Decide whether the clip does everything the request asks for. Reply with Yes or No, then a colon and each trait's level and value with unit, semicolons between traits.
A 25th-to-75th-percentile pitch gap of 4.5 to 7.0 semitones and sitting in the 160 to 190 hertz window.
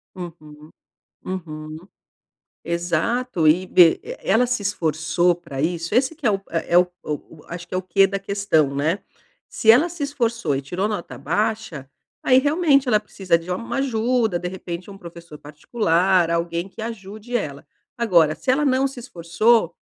Yes: wide, 5.5 semitones; medium, 185 Hz